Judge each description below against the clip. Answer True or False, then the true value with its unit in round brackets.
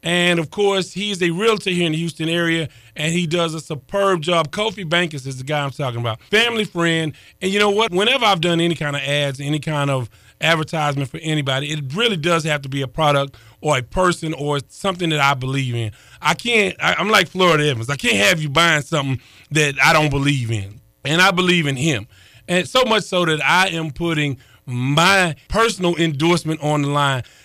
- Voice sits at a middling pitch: True (160 Hz)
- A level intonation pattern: False (3.9 semitones)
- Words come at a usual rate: False (215 wpm)